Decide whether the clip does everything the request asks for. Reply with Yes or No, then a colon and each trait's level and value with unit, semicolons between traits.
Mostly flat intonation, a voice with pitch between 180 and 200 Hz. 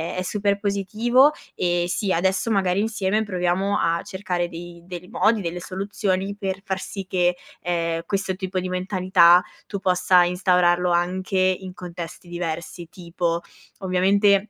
Yes: narrow, 2.0 semitones; medium, 185 Hz